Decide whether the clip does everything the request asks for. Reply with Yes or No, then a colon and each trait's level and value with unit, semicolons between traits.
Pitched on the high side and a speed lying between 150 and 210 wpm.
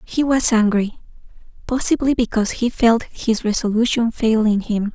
No: high, 230 Hz; slow, 135 wpm